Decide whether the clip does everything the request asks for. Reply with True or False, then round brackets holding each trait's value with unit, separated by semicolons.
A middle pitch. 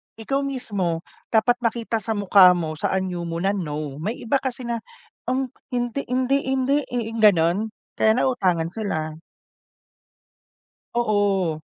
False (215 Hz)